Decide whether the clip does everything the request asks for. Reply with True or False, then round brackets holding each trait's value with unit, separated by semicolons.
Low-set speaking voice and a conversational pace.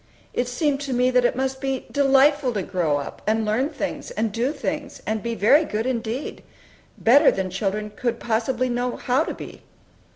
False (245 Hz; 190 wpm)